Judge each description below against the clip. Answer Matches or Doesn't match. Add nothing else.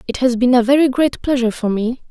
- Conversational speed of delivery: Doesn't match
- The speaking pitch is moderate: Doesn't match